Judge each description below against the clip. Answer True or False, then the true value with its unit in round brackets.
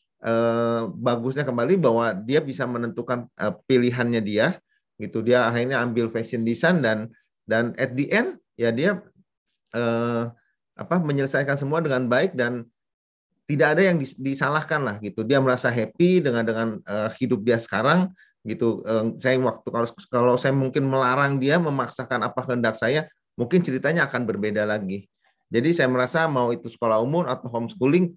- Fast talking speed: True (160 wpm)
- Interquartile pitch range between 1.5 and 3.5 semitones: True (3.2 semitones)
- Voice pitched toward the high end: False (125 Hz)